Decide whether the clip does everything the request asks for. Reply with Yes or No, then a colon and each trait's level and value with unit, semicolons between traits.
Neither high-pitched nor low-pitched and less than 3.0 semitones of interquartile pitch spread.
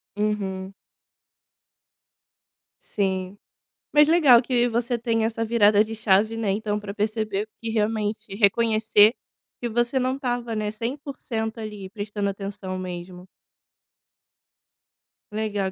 No: high, 215 Hz; narrow, 2.4 semitones